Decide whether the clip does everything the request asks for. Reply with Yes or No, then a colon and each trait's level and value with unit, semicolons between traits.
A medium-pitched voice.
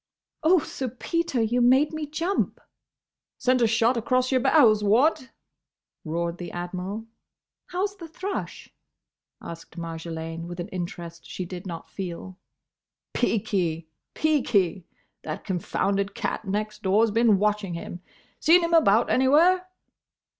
No: high, 215 Hz